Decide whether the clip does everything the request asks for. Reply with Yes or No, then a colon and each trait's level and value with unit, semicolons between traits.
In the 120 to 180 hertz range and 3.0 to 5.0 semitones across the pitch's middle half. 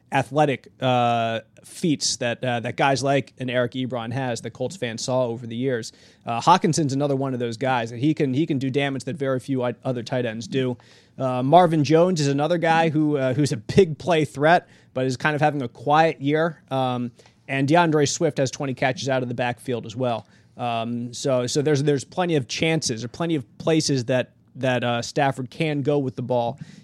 Yes: low, 135 Hz; average, 3.5 semitones